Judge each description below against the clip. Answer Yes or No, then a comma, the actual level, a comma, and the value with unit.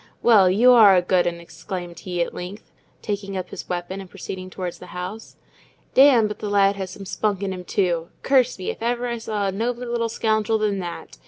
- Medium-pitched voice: No, high, 195 Hz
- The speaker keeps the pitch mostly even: No, average, 3.4 semitones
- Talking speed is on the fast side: Yes, fast, 220 wpm